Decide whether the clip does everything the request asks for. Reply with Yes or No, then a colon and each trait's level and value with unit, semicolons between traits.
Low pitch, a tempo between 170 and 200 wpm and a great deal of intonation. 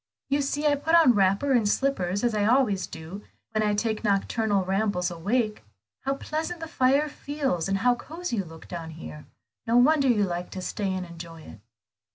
No: high, 215 Hz; average, 190 wpm; wide, 6.6 semitones